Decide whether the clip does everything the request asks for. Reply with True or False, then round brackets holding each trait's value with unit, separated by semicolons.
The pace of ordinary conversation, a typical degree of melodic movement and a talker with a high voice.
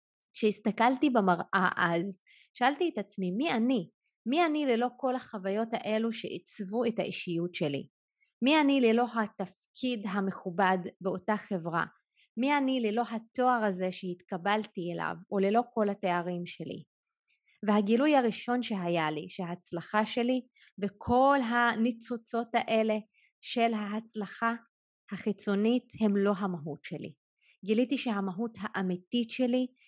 True (115 wpm; 4.1 semitones; 215 Hz)